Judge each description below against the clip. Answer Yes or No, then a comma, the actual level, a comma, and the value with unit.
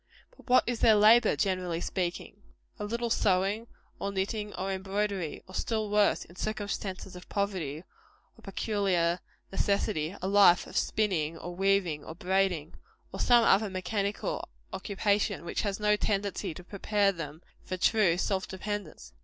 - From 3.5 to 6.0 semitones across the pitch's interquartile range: No, narrow, 2.5 semitones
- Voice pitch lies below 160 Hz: No, high, 195 Hz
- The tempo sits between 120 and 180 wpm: Yes, average, 150 wpm